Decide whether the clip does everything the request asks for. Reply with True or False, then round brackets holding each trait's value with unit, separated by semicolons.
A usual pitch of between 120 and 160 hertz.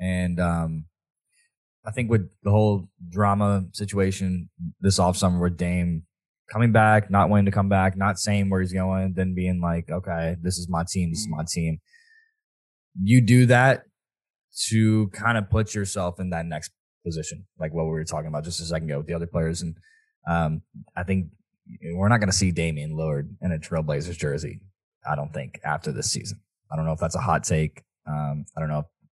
False (90 Hz)